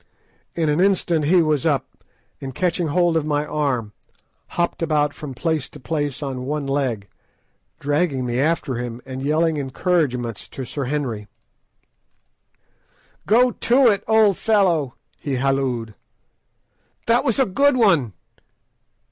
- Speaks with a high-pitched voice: No, medium, 150 Hz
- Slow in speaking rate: Yes, slow, 130 wpm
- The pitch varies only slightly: No, average, 4.6 semitones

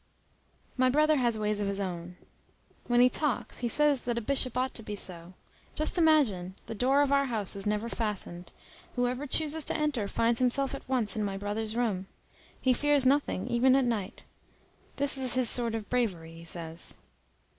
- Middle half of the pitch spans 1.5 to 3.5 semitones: No, average, 4.6 semitones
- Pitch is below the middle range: No, high, 240 Hz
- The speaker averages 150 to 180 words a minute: No, average, 190 wpm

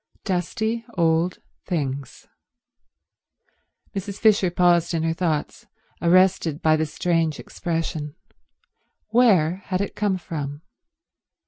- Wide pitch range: No, average, 2.9 semitones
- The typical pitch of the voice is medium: Yes, medium, 170 Hz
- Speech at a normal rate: No, slow, 100 wpm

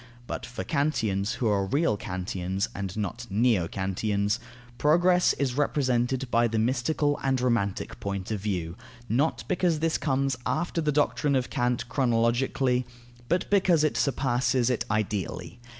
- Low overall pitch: Yes, low, 120 Hz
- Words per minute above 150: No, average, 145 wpm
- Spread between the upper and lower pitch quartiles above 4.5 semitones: Yes, wide, 5.5 semitones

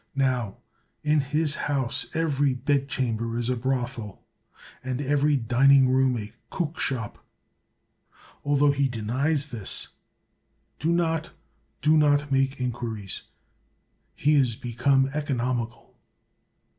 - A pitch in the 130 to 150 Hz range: Yes, low, 135 Hz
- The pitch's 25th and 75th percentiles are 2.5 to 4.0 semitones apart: Yes, average, 3.2 semitones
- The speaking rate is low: Yes, slow, 110 wpm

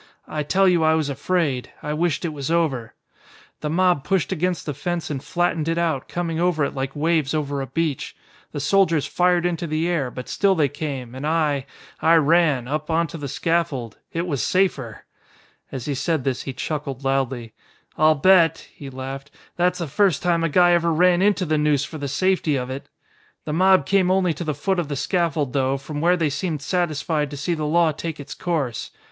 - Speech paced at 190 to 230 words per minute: Yes, fast, 205 wpm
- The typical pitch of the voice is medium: Yes, medium, 155 Hz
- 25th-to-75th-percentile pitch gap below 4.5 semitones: Yes, average, 3.6 semitones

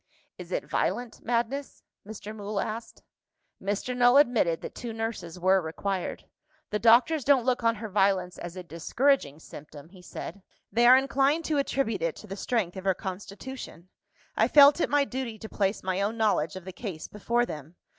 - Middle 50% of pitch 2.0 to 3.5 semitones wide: No, average, 4.8 semitones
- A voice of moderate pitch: No, high, 215 Hz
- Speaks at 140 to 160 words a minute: No, average, 185 wpm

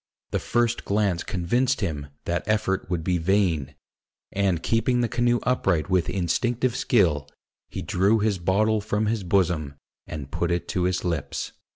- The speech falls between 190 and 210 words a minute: No, average, 160 wpm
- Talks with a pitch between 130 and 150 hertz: No, very low, 95 Hz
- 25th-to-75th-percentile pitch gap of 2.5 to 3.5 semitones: No, average, 4.2 semitones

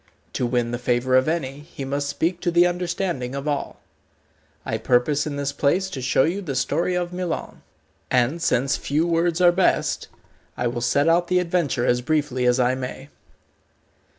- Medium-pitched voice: Yes, medium, 145 Hz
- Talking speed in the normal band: Yes, average, 180 wpm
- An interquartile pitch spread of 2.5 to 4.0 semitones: No, average, 5.2 semitones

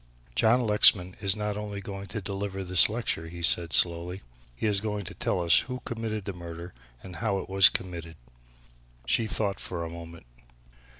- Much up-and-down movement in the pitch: No, average, 3.5 semitones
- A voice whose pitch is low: Yes, very low, 95 Hz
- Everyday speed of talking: Yes, average, 180 wpm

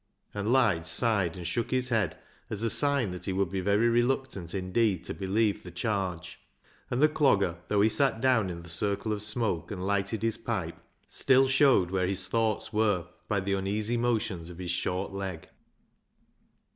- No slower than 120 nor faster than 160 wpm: No, average, 185 wpm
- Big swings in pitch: No, average, 3.8 semitones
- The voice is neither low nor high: No, low, 100 Hz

